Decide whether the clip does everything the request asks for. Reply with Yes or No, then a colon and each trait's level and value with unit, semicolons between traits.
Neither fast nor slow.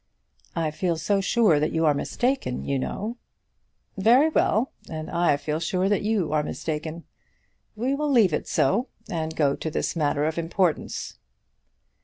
Yes: average, 160 wpm